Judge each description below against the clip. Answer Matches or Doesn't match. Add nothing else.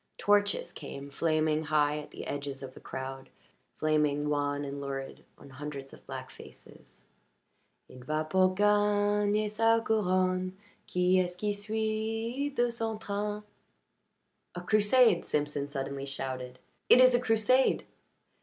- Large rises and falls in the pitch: Matches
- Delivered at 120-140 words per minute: Matches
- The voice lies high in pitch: Doesn't match